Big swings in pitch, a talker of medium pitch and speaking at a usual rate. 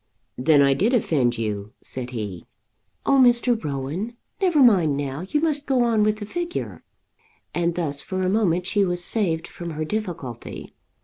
Yes: wide, 8.2 semitones; medium, 180 Hz; average, 170 wpm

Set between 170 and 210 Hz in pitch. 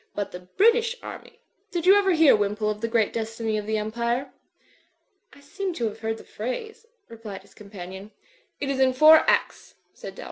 No: high, 230 Hz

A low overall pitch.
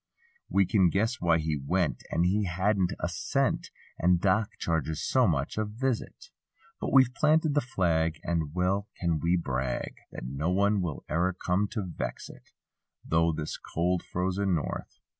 Yes: very low, 90 Hz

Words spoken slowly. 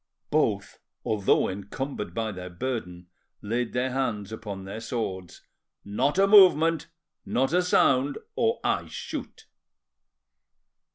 Yes: slow, 115 wpm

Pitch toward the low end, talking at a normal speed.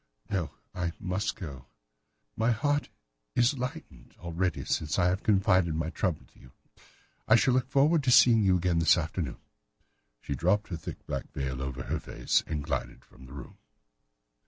Yes: very low, 90 Hz; average, 170 wpm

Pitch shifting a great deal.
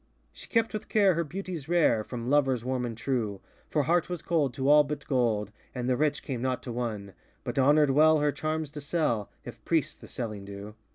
No: average, 4.7 semitones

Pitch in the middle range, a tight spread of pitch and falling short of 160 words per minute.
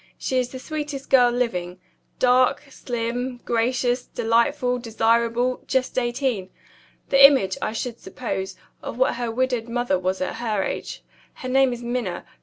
No: high, 245 Hz; narrow, 2.0 semitones; average, 150 wpm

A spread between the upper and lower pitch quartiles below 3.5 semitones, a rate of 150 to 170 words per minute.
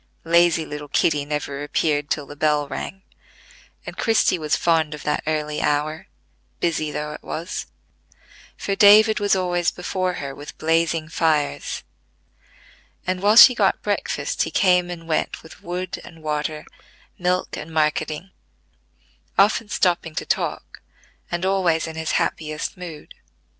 No: average, 3.1 semitones; average, 140 wpm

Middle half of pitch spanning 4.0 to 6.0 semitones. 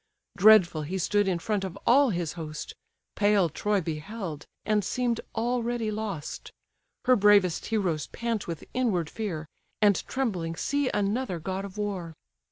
Yes: average, 4.5 semitones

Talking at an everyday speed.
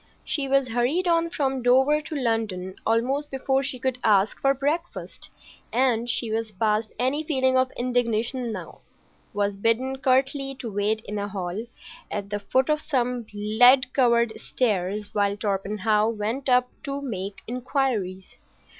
Yes: average, 145 wpm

